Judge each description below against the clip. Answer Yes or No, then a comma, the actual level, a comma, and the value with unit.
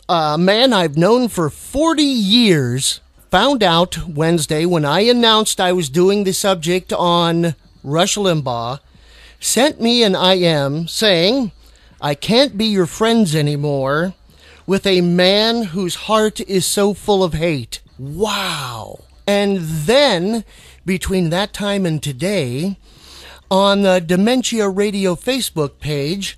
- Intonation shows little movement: No, average, 4.1 semitones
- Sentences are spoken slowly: Yes, slow, 125 wpm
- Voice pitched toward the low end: No, medium, 185 Hz